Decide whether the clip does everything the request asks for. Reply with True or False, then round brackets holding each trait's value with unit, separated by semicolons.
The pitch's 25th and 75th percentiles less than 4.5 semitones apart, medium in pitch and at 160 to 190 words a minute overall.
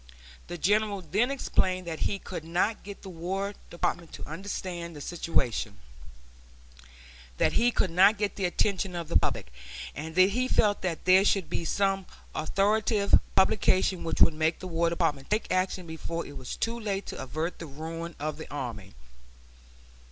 True (3.5 semitones; 180 Hz; 170 wpm)